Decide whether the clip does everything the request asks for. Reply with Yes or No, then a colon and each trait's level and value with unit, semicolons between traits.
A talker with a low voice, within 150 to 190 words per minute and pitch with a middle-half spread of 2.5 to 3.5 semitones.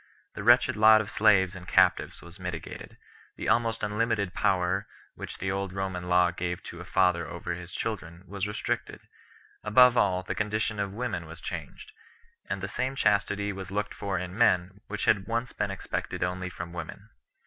Yes: very low, 95 Hz; average, 180 wpm; average, 3.0 semitones